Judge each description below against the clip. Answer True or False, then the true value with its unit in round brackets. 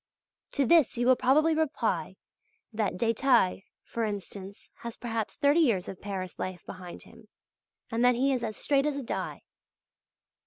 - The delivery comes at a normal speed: True (160 wpm)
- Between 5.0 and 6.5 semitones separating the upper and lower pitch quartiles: True (5.3 semitones)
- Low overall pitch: False (235 Hz)